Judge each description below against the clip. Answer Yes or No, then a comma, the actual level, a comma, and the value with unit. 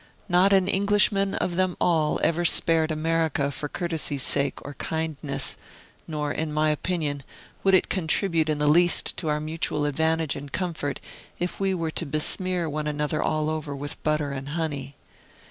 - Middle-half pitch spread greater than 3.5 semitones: No, average, 2.8 semitones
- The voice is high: No, medium, 155 Hz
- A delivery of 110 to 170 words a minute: Yes, average, 165 wpm